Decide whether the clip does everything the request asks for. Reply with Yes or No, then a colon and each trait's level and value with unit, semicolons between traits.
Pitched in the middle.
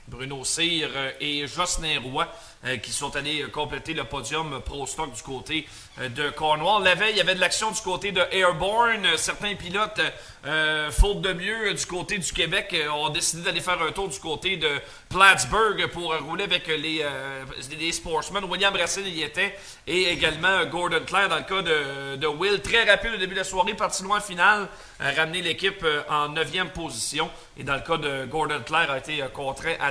Yes: medium, 160 Hz